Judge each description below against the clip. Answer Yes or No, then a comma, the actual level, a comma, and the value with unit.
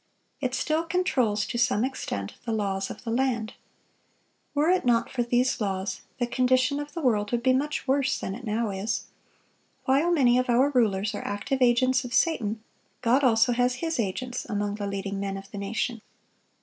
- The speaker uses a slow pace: No, average, 190 wpm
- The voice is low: No, high, 240 Hz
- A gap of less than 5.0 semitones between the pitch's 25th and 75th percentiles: Yes, average, 4.0 semitones